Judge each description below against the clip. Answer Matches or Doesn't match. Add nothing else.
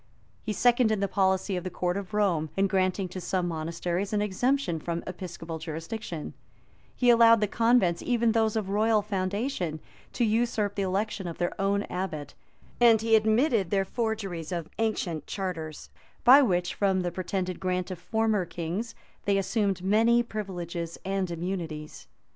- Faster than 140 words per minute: Matches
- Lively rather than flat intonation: Doesn't match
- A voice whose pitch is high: Matches